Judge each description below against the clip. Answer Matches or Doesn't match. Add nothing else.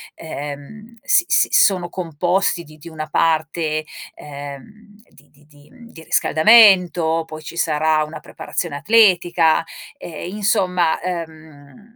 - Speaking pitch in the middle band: Matches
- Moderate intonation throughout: Matches